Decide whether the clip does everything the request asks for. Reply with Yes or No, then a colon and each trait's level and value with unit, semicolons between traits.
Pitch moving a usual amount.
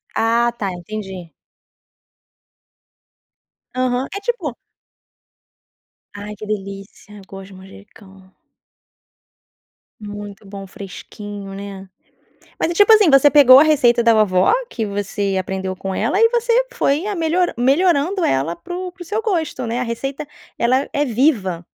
No: wide, 7.8 semitones